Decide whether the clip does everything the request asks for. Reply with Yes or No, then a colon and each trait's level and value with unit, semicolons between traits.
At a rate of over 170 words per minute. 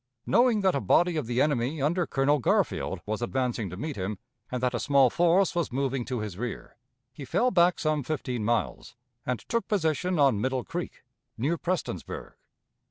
Yes: average, 180 wpm